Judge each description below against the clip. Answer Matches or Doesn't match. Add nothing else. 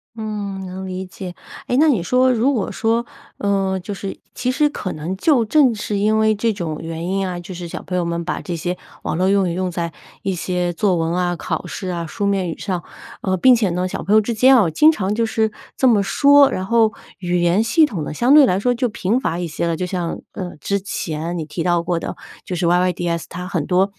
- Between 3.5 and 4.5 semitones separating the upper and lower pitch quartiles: Matches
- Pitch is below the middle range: Doesn't match